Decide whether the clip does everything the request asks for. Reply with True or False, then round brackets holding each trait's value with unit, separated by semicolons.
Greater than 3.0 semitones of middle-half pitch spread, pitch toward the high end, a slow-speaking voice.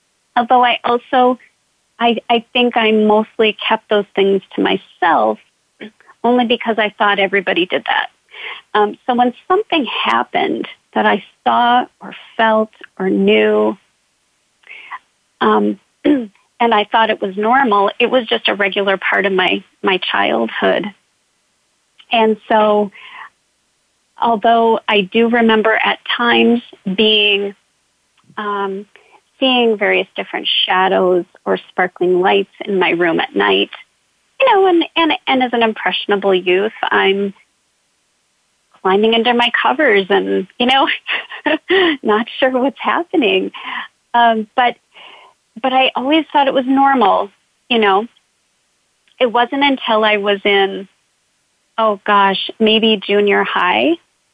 True (4.1 semitones; 225 Hz; 125 wpm)